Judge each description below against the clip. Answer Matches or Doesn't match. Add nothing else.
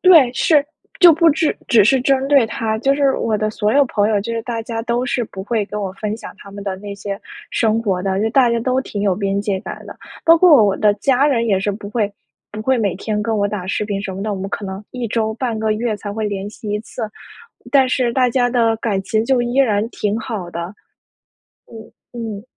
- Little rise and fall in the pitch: Doesn't match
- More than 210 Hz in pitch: Matches